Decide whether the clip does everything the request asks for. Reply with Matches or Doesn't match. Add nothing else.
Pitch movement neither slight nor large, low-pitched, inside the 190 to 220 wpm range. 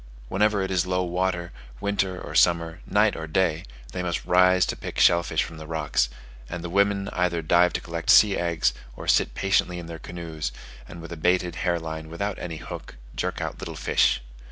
Doesn't match